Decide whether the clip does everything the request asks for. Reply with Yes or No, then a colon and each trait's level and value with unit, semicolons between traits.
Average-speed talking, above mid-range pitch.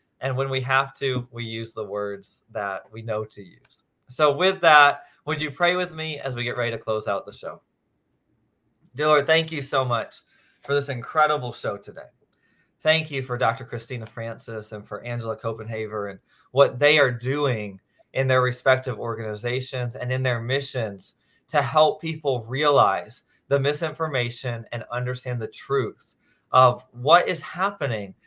No: average, 165 wpm; low, 130 Hz